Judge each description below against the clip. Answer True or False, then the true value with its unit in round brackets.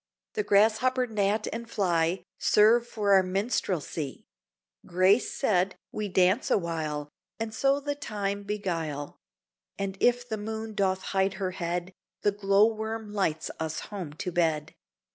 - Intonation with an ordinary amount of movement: True (3.6 semitones)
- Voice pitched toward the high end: True (200 Hz)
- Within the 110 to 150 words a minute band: True (140 wpm)